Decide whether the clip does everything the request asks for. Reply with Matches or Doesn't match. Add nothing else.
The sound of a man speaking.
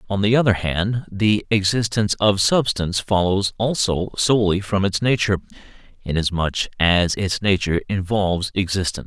Matches